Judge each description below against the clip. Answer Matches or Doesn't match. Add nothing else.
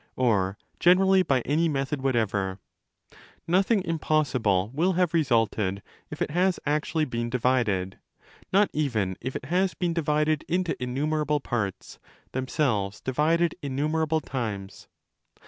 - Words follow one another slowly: Matches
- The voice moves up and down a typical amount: Doesn't match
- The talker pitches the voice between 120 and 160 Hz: Matches